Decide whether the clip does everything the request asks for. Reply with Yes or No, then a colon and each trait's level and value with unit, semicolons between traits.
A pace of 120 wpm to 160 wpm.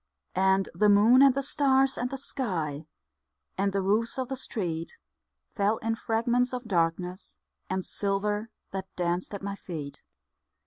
Yes: average, 150 wpm